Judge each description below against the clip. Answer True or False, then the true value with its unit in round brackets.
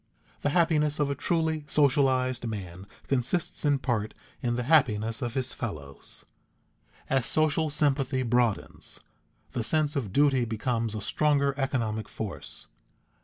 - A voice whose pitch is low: True (130 Hz)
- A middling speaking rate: False (130 wpm)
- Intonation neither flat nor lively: True (4.5 semitones)